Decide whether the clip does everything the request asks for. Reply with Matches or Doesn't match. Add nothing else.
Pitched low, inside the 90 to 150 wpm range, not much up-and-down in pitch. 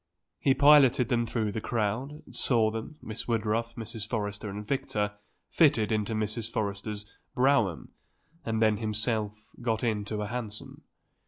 Matches